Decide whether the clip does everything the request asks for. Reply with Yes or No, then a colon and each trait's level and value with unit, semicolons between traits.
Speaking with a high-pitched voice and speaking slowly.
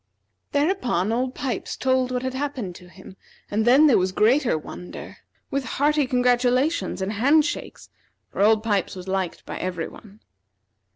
No: high, 245 Hz; average, 160 wpm